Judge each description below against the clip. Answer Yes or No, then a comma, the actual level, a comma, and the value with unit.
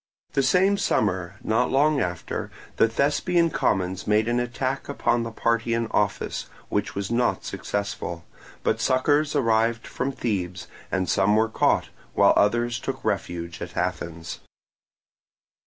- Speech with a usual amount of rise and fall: Yes, average, 5.0 semitones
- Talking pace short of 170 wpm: Yes, average, 140 wpm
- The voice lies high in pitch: No, low, 115 Hz